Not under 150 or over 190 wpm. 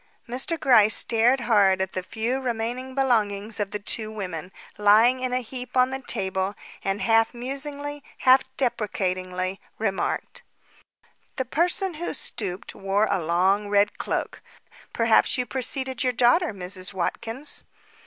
No: average, 140 wpm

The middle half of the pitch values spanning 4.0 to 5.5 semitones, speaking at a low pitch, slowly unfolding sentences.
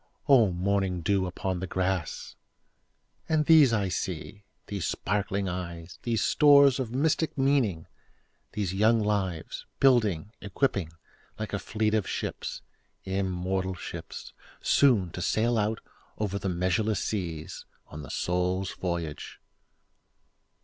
No: average, 3.5 semitones; low, 100 Hz; slow, 100 wpm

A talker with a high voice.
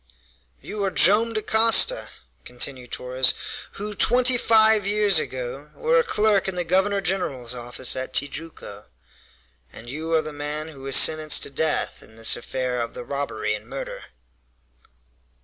No: medium, 155 Hz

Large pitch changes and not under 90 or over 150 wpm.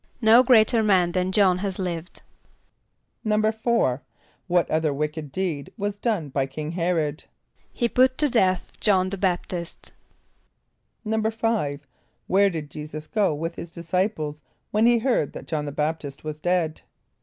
Yes: wide, 5.7 semitones; average, 145 wpm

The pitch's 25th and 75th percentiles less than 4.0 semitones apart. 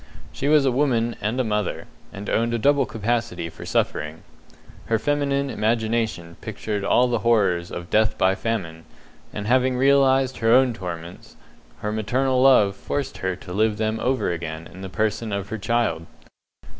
No: average, 4.6 semitones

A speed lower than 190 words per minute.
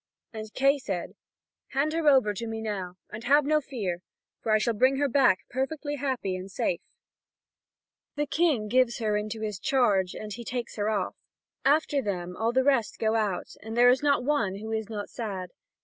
No: average, 195 wpm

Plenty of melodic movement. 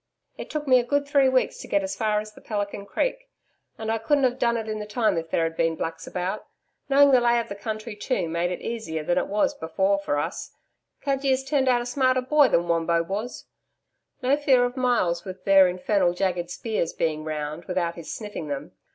Yes: wide, 6.4 semitones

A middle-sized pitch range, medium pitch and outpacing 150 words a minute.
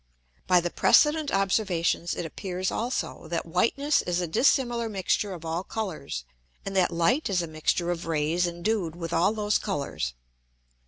Yes: average, 4.0 semitones; medium, 180 Hz; average, 160 wpm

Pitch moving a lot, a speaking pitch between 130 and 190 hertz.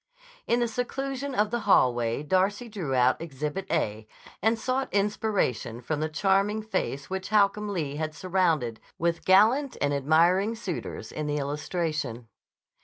Yes: wide, 6.2 semitones; medium, 185 Hz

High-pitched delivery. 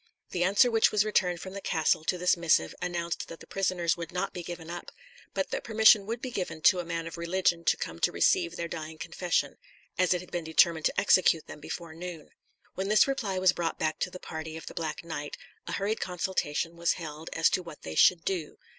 No: medium, 175 Hz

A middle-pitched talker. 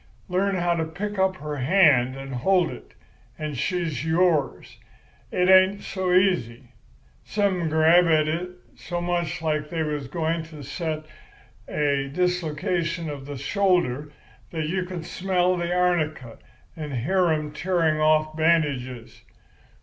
Yes: medium, 165 Hz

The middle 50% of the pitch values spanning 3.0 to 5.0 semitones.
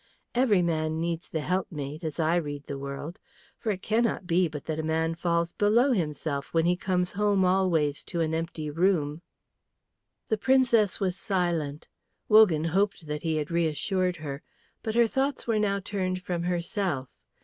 Yes: average, 4.0 semitones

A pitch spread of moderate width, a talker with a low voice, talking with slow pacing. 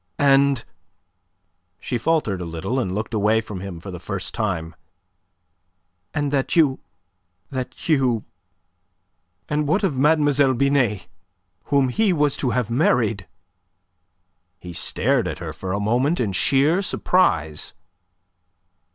No: wide, 6.2 semitones; low, 125 Hz; slow, 125 wpm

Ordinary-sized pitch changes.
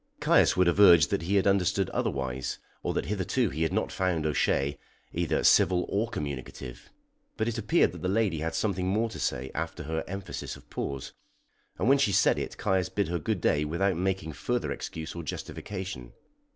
Yes: average, 4.1 semitones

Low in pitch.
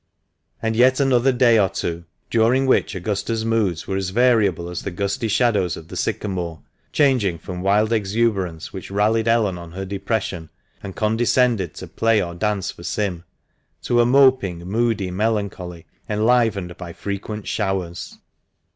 Yes: low, 105 Hz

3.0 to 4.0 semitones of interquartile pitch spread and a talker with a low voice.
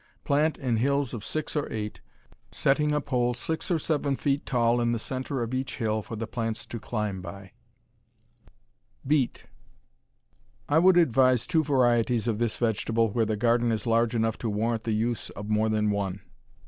Yes: average, 3.6 semitones; low, 120 Hz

